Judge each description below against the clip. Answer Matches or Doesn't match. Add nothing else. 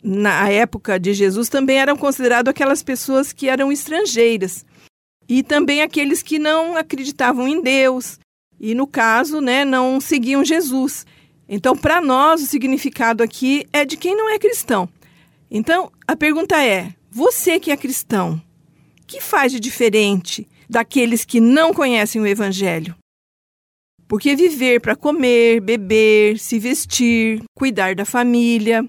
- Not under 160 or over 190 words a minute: Doesn't match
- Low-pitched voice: Doesn't match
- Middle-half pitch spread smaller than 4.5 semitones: Doesn't match